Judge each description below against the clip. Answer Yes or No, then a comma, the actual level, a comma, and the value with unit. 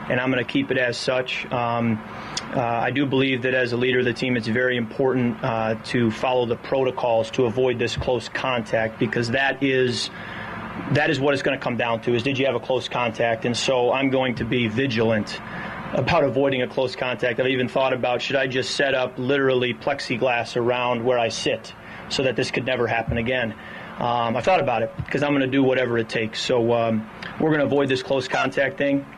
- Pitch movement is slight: Yes, narrow, 2.0 semitones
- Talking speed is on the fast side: Yes, fast, 225 wpm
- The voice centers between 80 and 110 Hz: No, low, 125 Hz